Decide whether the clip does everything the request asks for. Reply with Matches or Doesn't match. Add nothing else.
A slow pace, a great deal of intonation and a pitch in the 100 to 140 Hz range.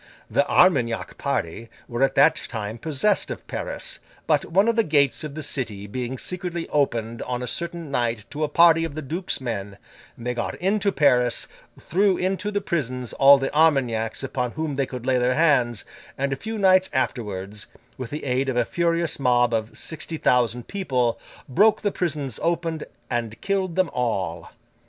Doesn't match